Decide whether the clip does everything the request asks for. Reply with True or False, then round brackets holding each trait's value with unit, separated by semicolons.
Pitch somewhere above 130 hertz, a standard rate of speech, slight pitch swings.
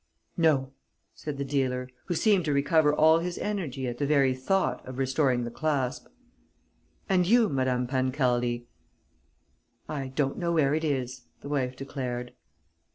False (140 Hz; 150 wpm; 3.4 semitones)